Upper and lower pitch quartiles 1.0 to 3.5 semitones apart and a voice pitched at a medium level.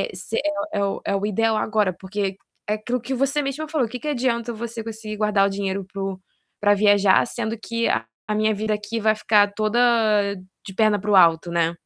No: narrow, 2.4 semitones; high, 215 Hz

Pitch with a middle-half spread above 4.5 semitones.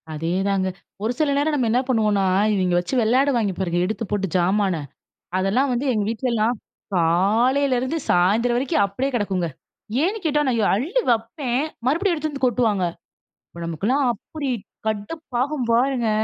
Yes: wide, 5.4 semitones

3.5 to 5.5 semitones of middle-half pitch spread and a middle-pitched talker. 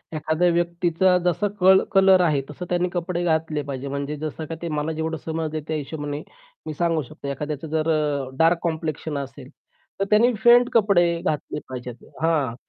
No: average, 2.8 semitones; medium, 160 Hz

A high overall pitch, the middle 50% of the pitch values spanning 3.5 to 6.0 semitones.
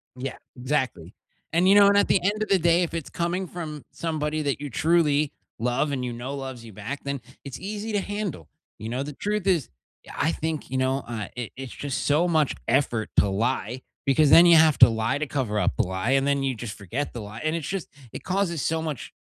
No: medium, 140 Hz; average, 5.2 semitones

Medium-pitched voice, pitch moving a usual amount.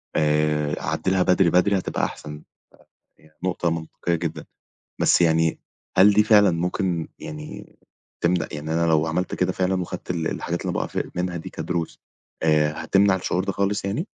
No: very low, 90 Hz; average, 3.0 semitones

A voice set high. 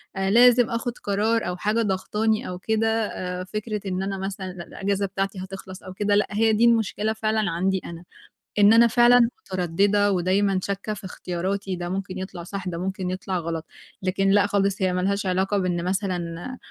Yes: high, 195 Hz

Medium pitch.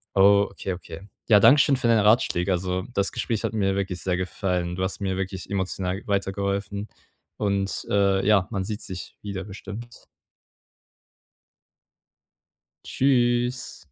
No: low, 100 Hz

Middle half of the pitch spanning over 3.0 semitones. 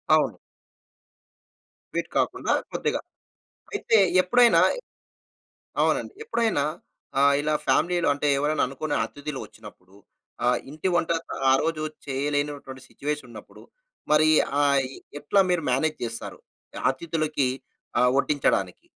No: average, 2.7 semitones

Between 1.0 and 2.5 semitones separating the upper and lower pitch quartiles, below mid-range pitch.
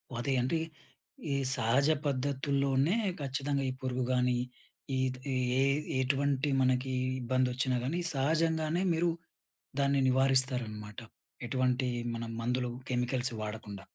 Yes: narrow, 1.9 semitones; low, 130 Hz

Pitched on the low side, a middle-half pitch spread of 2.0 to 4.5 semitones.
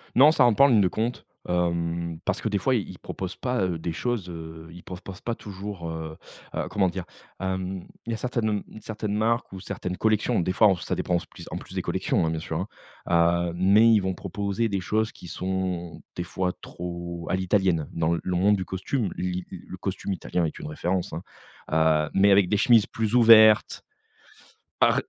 Yes: very low, 95 Hz; average, 3.7 semitones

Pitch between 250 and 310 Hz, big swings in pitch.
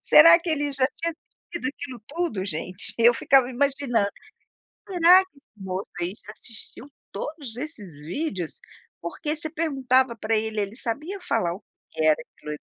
Yes: very high, 255 Hz; wide, 7.0 semitones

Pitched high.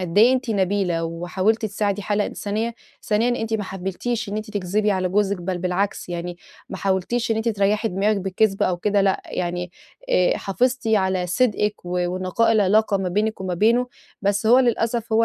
Yes: high, 205 Hz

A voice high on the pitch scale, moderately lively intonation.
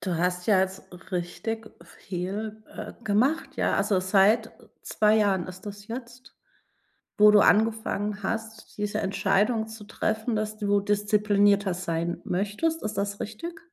No: high, 210 Hz; narrow, 2.1 semitones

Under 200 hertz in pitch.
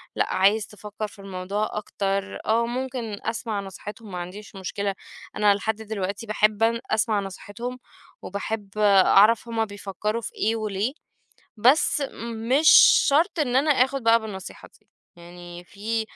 No: high, 210 Hz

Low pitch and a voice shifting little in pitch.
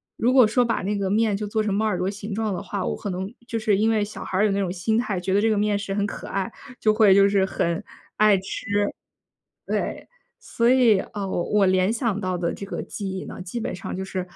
No: high, 205 Hz; narrow, 2.2 semitones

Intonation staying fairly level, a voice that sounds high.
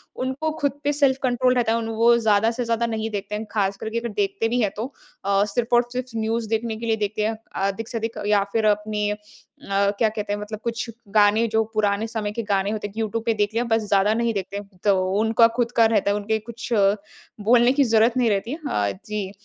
Yes: narrow, 2.1 semitones; high, 220 Hz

